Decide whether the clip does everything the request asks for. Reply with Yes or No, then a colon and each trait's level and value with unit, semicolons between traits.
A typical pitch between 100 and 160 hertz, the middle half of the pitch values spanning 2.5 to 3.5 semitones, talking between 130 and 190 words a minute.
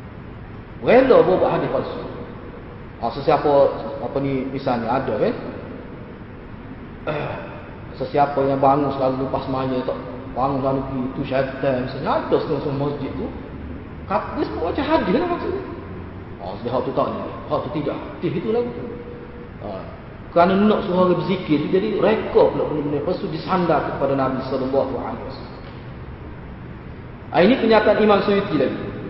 Yes: low, 135 Hz; average, 3.1 semitones; average, 140 wpm